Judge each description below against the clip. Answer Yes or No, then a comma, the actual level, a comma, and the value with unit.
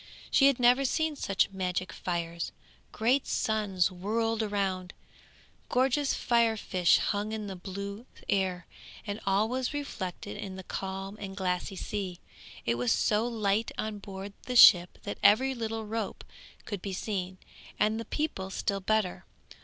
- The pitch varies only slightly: No, average, 3.1 semitones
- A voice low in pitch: No, high, 205 Hz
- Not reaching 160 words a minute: Yes, average, 150 wpm